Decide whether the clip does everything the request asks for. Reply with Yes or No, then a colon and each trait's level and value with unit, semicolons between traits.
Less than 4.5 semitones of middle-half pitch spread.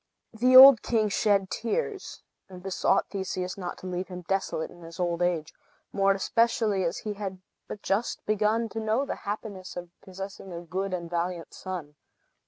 Yes: average, 3.1 semitones